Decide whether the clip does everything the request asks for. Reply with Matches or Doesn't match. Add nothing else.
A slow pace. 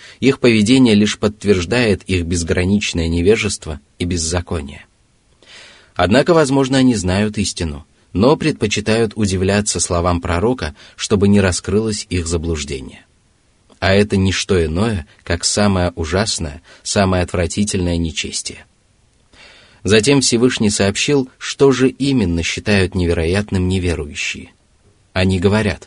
Matches